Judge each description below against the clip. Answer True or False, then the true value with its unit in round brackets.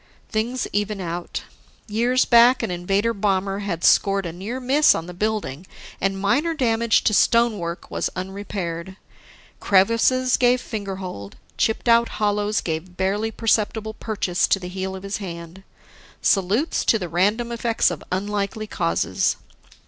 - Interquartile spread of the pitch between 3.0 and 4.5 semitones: True (3.6 semitones)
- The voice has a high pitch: True (205 Hz)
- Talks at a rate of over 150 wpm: False (140 wpm)